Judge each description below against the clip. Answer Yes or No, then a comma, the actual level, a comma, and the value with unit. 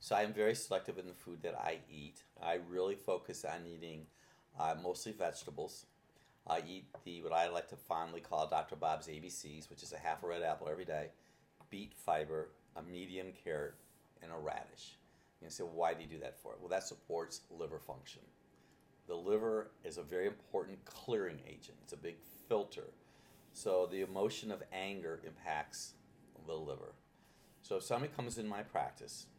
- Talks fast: No, average, 185 wpm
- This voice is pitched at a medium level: No, very low, 95 Hz